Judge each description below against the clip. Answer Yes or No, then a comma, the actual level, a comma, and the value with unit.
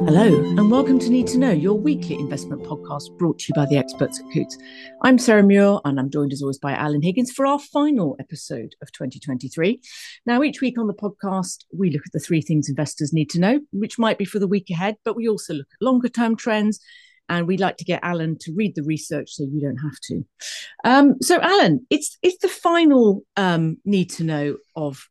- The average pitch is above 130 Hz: Yes, medium, 185 Hz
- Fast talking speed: Yes, fast, 220 wpm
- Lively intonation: Yes, wide, 8.2 semitones